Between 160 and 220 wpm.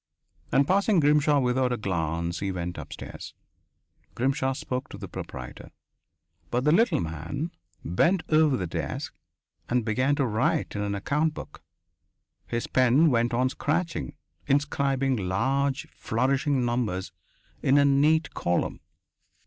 No: slow, 135 wpm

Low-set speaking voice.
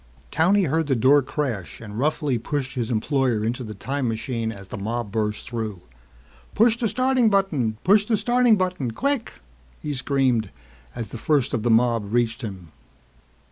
Yes: low, 130 Hz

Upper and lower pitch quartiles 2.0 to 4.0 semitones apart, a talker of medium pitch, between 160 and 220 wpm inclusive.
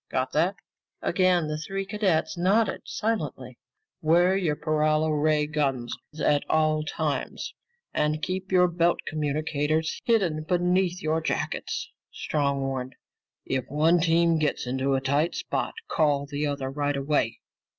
No: average, 3.3 semitones; medium, 155 Hz; slow, 135 wpm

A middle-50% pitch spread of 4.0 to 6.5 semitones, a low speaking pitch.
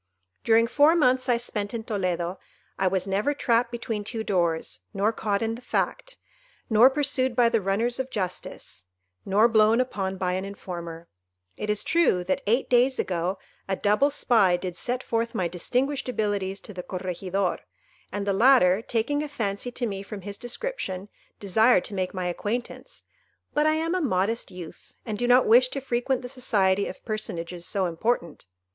No: average, 4.6 semitones; high, 215 Hz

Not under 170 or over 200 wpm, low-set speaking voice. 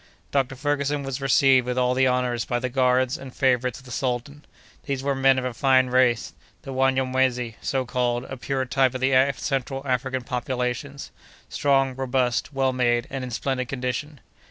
Yes: average, 180 wpm; low, 130 Hz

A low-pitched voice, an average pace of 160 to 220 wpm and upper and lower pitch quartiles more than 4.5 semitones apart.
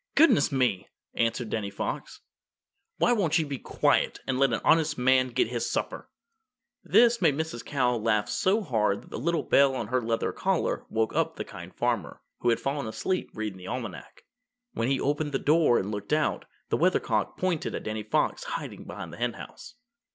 Yes: low, 125 Hz; average, 185 wpm; average, 5.3 semitones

